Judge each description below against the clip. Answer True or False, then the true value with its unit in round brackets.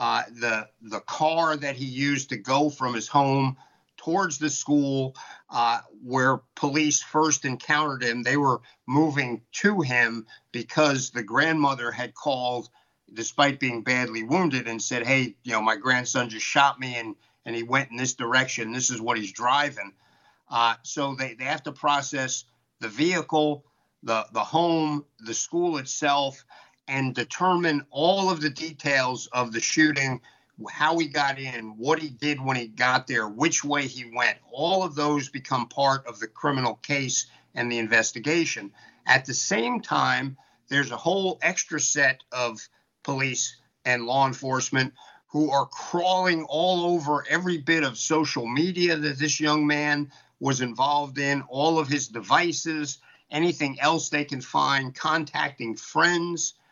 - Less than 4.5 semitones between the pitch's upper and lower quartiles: True (3.5 semitones)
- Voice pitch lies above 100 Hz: True (140 Hz)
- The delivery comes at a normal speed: True (160 wpm)